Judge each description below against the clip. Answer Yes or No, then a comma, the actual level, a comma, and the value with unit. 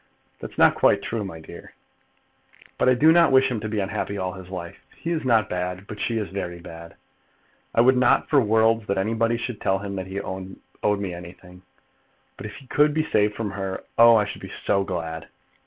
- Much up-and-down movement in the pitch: No, average, 3.7 semitones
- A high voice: No, low, 105 Hz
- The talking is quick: Yes, fast, 210 wpm